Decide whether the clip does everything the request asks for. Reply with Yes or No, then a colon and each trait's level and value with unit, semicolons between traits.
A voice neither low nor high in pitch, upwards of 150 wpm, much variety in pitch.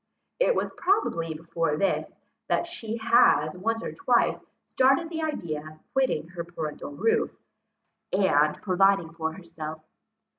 No: medium, 175 Hz; slow, 135 wpm; wide, 6.6 semitones